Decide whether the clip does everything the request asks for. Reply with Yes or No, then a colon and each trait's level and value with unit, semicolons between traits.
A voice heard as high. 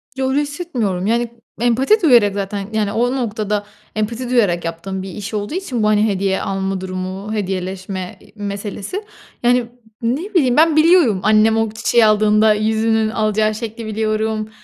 Yes: high, 215 Hz